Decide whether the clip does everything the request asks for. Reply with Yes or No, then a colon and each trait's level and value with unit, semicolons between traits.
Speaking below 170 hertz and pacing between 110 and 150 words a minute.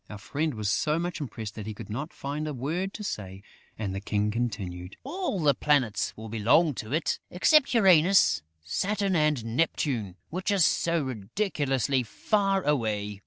No: medium, 140 Hz; average, 165 wpm